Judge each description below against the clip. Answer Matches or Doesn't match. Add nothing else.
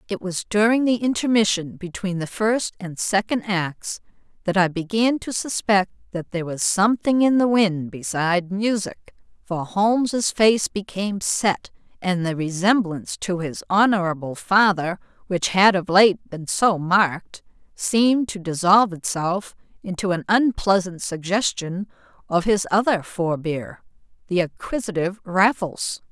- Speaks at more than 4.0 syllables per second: Matches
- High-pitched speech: Matches